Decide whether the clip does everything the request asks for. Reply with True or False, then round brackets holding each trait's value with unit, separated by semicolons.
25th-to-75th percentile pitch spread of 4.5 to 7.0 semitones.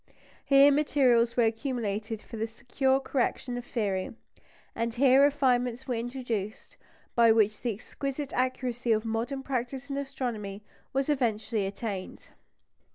False (3.2 semitones)